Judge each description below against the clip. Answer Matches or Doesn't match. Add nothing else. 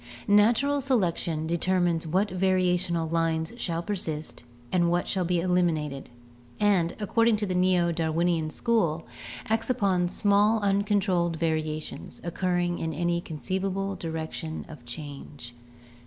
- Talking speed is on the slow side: Matches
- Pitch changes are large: Doesn't match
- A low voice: Doesn't match